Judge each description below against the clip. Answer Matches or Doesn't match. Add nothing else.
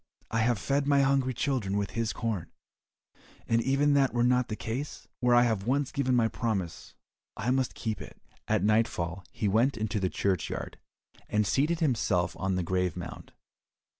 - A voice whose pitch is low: Matches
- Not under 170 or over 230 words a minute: Matches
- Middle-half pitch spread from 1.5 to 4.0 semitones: Doesn't match